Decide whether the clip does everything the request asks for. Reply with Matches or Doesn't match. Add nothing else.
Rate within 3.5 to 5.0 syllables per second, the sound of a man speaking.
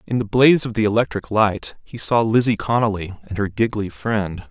Doesn't match